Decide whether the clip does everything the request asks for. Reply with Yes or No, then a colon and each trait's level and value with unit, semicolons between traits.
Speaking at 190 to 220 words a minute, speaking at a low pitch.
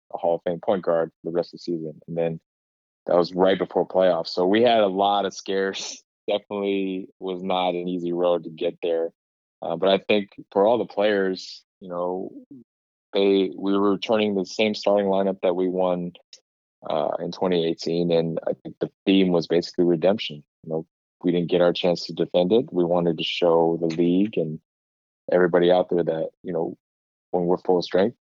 Yes: average, 200 wpm; very low, 90 Hz